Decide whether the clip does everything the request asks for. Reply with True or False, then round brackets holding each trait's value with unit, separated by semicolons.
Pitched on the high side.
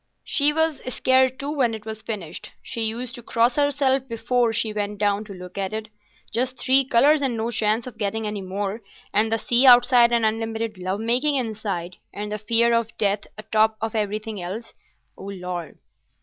True (225 Hz)